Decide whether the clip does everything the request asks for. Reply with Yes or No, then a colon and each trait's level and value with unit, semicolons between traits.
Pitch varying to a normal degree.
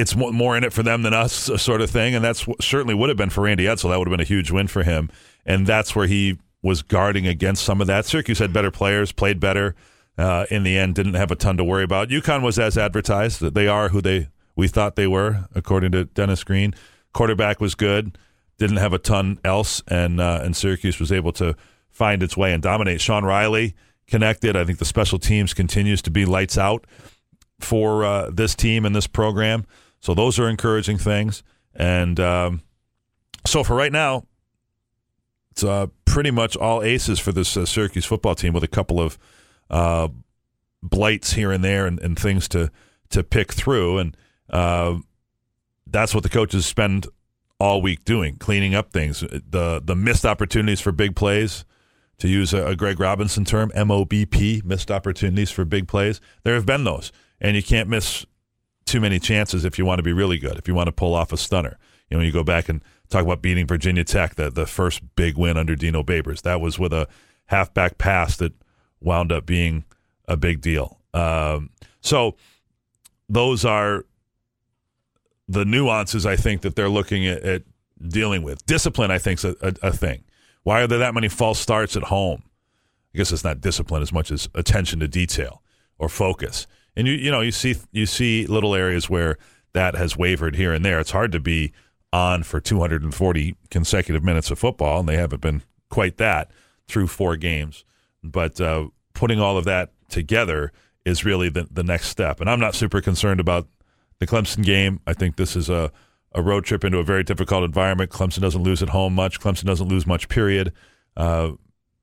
Yes: average, 3.4 semitones